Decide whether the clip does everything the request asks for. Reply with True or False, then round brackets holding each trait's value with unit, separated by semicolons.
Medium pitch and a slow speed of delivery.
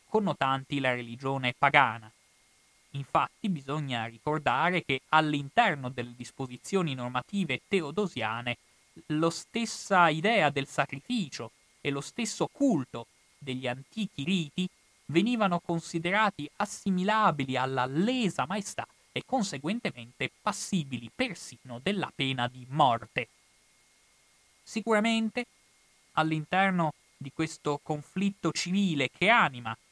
True (155 Hz; 95 wpm)